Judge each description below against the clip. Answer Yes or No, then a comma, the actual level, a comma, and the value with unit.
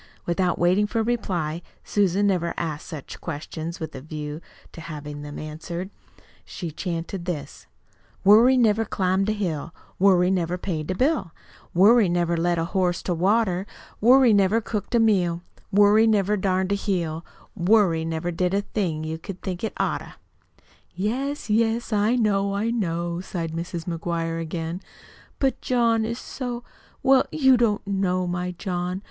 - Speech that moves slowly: No, average, 155 wpm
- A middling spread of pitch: Yes, average, 3.9 semitones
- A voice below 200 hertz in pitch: Yes, medium, 185 Hz